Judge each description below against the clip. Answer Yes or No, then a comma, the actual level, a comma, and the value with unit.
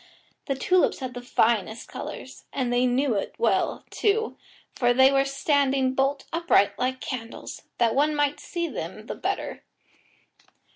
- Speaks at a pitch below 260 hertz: No, very high, 265 Hz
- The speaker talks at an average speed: Yes, average, 150 wpm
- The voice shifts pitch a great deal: No, average, 2.8 semitones